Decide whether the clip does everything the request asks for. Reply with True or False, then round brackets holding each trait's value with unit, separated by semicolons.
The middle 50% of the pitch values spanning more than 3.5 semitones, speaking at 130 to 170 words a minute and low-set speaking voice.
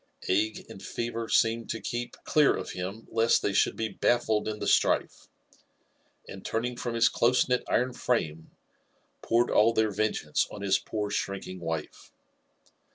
False (3.1 semitones; 155 wpm; 110 Hz)